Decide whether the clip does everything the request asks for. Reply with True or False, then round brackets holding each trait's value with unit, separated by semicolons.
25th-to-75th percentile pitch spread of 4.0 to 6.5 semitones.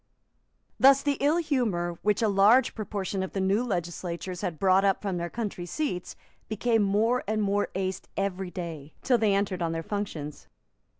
False (3.6 semitones)